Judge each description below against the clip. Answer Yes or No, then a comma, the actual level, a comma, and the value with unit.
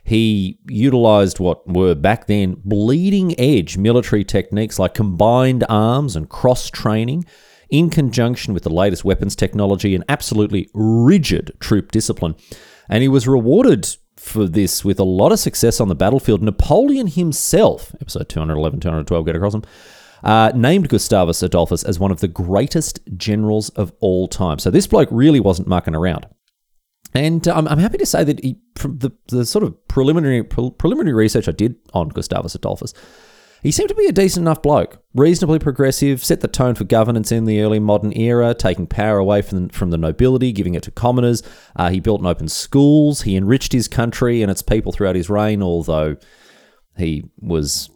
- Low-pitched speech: Yes, low, 110 Hz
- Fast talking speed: No, average, 180 wpm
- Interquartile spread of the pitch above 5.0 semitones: Yes, wide, 5.5 semitones